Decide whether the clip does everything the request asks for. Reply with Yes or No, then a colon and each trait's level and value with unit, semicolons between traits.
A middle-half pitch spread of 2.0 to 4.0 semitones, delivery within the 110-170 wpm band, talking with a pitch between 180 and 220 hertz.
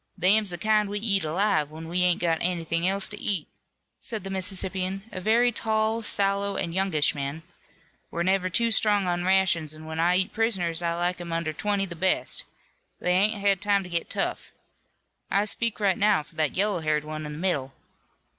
No: average, 3.3 semitones; average, 200 wpm; medium, 185 Hz